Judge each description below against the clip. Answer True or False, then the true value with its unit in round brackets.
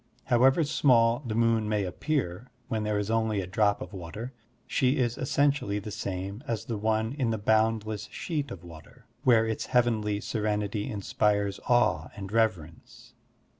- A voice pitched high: False (110 Hz)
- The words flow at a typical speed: True (160 wpm)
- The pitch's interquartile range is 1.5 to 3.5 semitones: True (2.6 semitones)